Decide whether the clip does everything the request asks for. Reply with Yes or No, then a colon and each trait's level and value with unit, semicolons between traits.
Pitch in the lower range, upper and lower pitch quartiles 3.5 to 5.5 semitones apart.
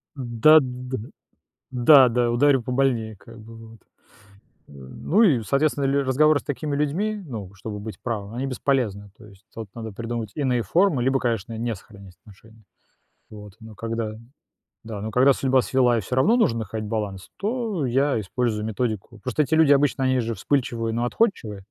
Yes: low, 120 Hz; average, 3.9 semitones